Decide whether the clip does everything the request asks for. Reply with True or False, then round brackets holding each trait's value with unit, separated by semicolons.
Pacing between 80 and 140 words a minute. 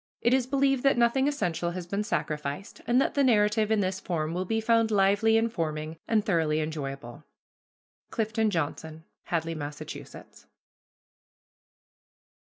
True (135 wpm)